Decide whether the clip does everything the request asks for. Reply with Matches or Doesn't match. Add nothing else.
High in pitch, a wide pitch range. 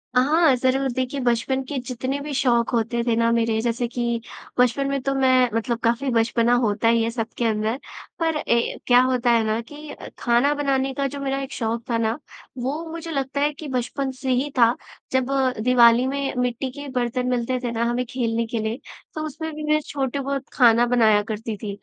Doesn't match